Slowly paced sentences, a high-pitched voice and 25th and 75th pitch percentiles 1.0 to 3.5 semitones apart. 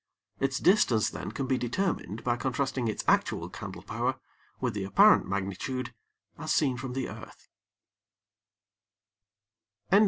No: slow, 125 wpm; low, 125 Hz; average, 3.1 semitones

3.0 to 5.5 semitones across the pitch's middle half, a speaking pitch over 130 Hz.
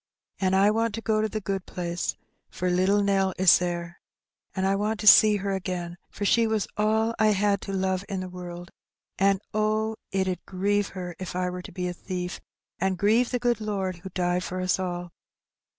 No: narrow, 2.6 semitones; high, 190 Hz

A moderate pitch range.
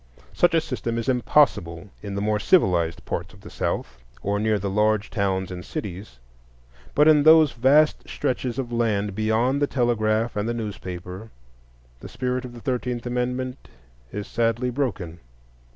Yes: average, 4.1 semitones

